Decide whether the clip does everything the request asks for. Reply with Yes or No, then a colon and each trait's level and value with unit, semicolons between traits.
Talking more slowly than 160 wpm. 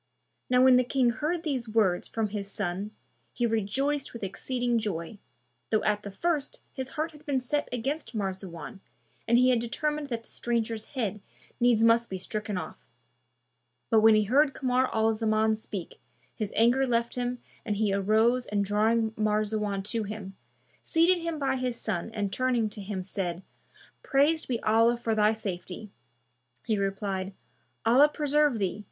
No: average, 165 wpm